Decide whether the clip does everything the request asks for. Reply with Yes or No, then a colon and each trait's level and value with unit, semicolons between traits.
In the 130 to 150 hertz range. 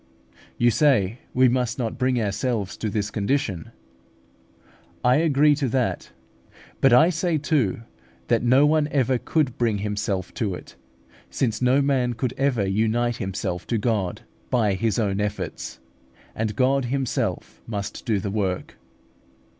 No: low, 120 Hz